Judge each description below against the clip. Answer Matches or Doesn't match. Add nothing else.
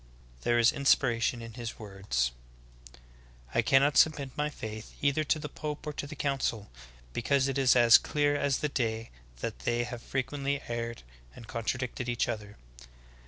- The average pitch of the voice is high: Doesn't match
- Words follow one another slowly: Doesn't match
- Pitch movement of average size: Matches